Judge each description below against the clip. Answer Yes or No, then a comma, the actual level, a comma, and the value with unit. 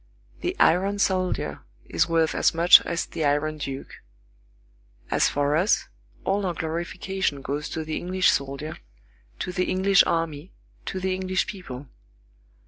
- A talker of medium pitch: Yes, medium, 170 Hz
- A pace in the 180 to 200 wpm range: No, average, 140 wpm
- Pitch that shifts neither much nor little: Yes, average, 3.7 semitones